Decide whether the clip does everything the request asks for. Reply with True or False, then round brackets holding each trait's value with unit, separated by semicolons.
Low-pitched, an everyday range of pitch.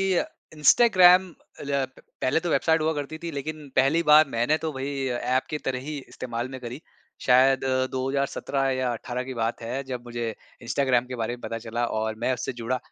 True (130 Hz; 3.4 semitones)